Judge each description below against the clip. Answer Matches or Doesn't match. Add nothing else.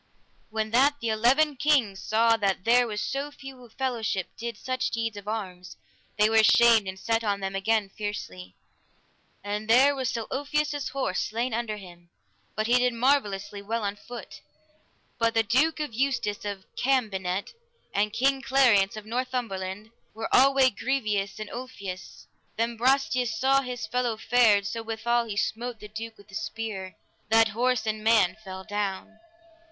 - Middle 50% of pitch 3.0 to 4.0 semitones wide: Matches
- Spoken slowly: Doesn't match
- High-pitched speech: Matches